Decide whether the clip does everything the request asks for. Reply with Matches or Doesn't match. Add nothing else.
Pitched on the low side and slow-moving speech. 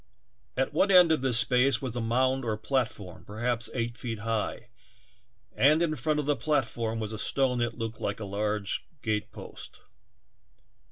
Doesn't match